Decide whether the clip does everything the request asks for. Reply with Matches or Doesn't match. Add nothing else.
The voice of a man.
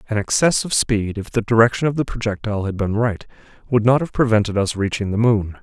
Matches